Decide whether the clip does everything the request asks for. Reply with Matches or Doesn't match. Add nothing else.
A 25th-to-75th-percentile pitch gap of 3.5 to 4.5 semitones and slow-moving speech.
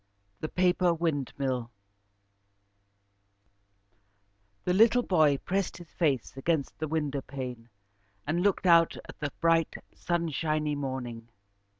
Matches